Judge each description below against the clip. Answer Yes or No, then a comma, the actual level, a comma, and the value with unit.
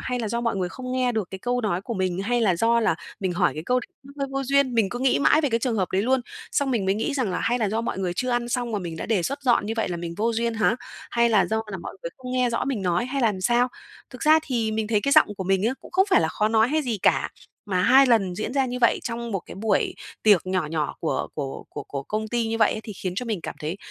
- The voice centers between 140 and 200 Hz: No, high, 225 Hz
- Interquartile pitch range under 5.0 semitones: Yes, average, 4.5 semitones